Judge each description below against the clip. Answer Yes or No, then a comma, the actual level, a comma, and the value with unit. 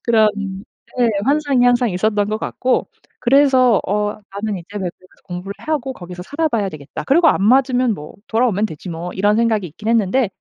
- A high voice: Yes, high, 220 Hz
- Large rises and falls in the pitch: No, average, 4.8 semitones